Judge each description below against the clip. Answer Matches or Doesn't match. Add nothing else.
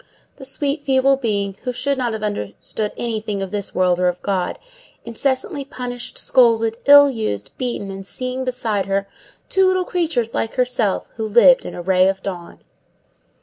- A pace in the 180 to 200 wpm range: Doesn't match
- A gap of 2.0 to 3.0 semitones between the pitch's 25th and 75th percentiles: Doesn't match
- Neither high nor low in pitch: Doesn't match